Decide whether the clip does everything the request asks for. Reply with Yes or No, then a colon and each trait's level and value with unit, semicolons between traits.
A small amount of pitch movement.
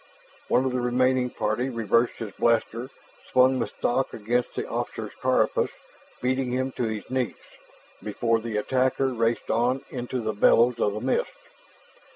Yes: narrow, 2.0 semitones